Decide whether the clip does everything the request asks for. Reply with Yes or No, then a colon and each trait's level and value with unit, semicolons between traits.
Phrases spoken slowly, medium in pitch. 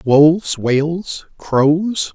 Yes: slow, 85 wpm; medium, 160 Hz